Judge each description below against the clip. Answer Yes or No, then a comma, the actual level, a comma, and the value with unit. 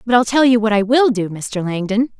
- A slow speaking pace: No, fast, 275 wpm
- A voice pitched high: Yes, high, 225 Hz